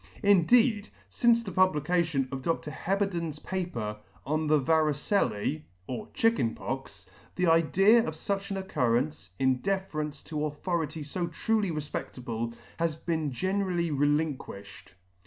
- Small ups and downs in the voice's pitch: No, wide, 5.4 semitones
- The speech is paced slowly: Yes, slow, 125 wpm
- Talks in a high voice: No, medium, 160 Hz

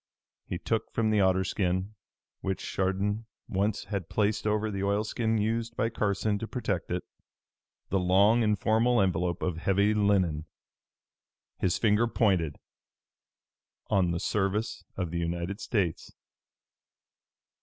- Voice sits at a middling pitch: No, low, 100 Hz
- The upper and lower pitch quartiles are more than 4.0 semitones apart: No, average, 2.8 semitones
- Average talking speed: No, slow, 130 wpm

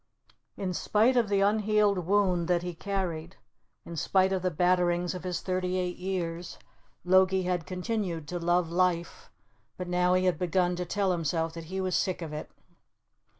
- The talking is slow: No, average, 175 wpm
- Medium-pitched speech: Yes, medium, 180 Hz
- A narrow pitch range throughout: Yes, narrow, 1.6 semitones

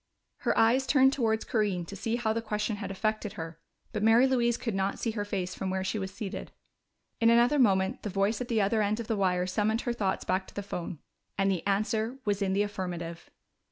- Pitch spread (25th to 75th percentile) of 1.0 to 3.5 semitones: Yes, average, 3.0 semitones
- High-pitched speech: Yes, high, 210 Hz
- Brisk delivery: Yes, fast, 225 wpm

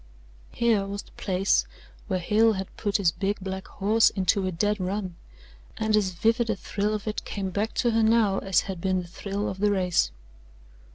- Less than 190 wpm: No, average, 195 wpm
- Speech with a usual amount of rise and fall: No, narrow, 2.2 semitones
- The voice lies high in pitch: Yes, high, 200 Hz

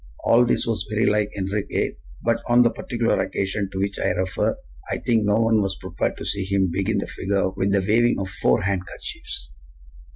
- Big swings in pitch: No, narrow, 2.6 semitones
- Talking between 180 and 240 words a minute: Yes, average, 195 wpm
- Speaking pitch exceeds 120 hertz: No, low, 100 Hz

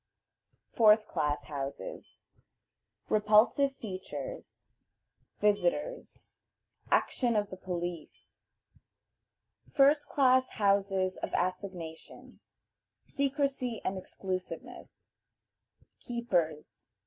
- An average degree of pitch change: No, wide, 6.0 semitones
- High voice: Yes, high, 205 Hz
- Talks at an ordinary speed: No, slow, 65 wpm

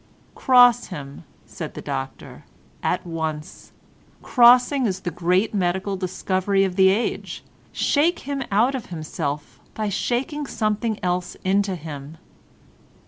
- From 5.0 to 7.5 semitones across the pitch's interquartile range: Yes, wide, 5.4 semitones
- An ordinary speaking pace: No, slow, 125 wpm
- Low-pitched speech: No, high, 190 Hz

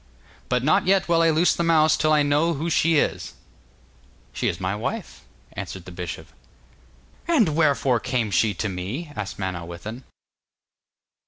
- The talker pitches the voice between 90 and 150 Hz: Yes, medium, 140 Hz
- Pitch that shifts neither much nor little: No, wide, 8.5 semitones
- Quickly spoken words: No, average, 155 wpm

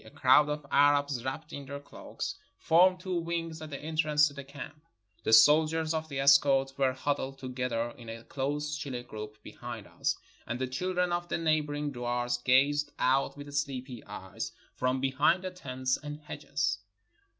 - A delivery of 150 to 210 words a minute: Yes, average, 175 wpm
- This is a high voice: No, medium, 140 Hz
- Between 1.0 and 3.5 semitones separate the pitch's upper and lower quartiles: Yes, average, 2.9 semitones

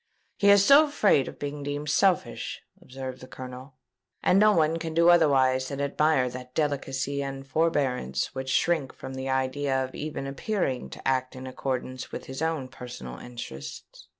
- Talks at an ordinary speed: Yes, average, 170 wpm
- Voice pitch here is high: No, low, 135 Hz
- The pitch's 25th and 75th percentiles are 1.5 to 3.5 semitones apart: Yes, average, 3.2 semitones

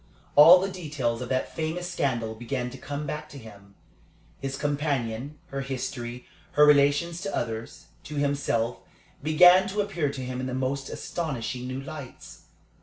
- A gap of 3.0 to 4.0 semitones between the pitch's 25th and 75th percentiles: Yes, average, 3.5 semitones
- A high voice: No, medium, 140 Hz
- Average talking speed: Yes, average, 160 wpm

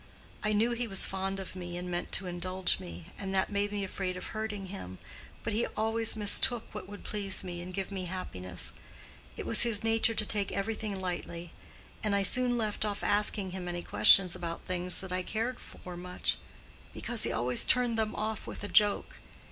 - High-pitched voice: Yes, high, 195 Hz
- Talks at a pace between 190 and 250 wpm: Yes, average, 200 wpm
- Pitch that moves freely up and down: No, average, 3.0 semitones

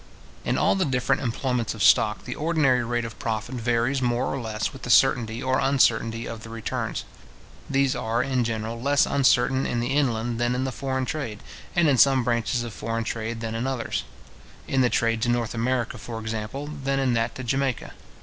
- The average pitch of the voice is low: Yes, low, 120 Hz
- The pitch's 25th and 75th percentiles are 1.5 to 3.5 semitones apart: Yes, average, 2.7 semitones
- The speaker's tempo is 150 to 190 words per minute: No, average, 200 wpm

